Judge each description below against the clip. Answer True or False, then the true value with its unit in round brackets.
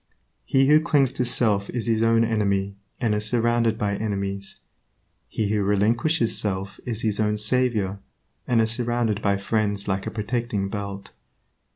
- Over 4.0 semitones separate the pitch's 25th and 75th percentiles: False (2.9 semitones)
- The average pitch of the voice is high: False (110 Hz)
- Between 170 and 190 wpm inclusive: False (160 wpm)